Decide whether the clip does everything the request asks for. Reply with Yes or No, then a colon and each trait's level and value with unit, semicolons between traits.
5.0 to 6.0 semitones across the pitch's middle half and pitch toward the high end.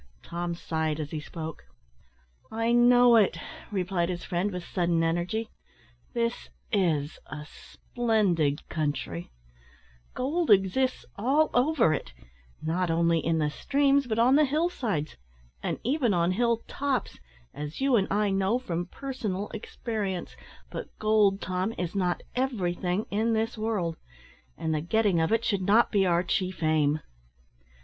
Yes: wide, 5.6 semitones; high, 195 Hz